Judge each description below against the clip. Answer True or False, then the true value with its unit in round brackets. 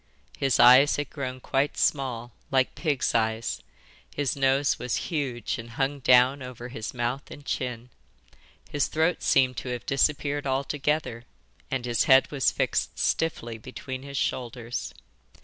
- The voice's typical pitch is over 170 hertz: False (130 Hz)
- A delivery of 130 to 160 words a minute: True (145 wpm)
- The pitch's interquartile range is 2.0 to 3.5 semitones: True (2.4 semitones)